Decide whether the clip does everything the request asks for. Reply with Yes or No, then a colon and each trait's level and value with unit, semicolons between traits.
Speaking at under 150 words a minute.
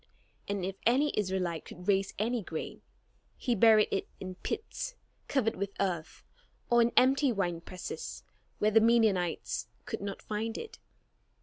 Yes: average, 140 wpm